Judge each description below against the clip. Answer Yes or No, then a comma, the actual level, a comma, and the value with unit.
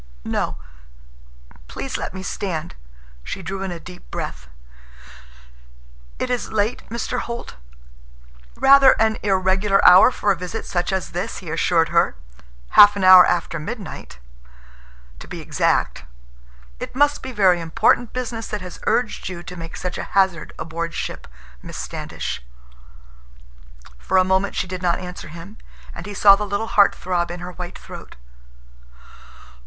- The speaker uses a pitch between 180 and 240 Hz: Yes, high, 190 Hz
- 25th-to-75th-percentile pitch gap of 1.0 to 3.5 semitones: Yes, average, 3.1 semitones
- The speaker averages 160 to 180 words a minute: No, average, 150 wpm